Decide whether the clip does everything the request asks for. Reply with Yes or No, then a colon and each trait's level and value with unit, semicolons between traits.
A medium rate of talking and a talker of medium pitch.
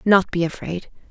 Yes: average, 165 wpm; medium, 180 Hz